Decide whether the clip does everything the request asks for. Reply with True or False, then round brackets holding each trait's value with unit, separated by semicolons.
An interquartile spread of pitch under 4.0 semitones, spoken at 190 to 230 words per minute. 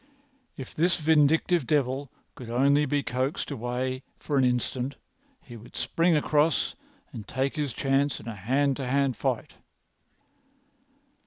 False (2.7 semitones; 140 wpm)